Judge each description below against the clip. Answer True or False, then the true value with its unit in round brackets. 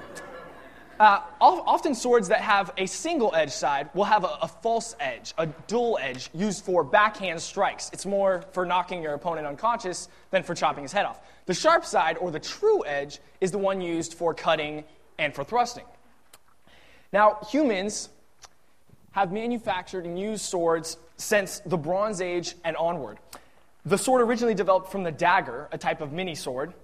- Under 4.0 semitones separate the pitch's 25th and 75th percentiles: False (4.3 semitones)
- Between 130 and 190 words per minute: True (170 wpm)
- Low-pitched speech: False (185 Hz)